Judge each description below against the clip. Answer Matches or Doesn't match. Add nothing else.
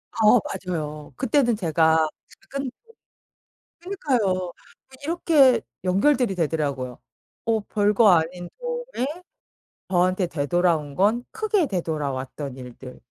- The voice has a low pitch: Doesn't match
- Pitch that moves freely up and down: Matches